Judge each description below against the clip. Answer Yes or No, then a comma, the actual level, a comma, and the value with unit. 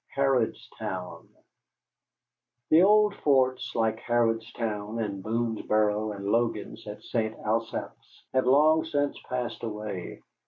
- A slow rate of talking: Yes, slow, 105 wpm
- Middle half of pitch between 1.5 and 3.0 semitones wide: No, average, 3.4 semitones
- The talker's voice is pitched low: Yes, low, 115 Hz